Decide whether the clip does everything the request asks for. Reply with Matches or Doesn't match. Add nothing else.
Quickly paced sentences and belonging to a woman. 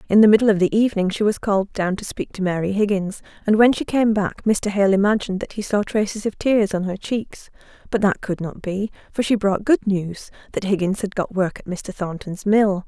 Matches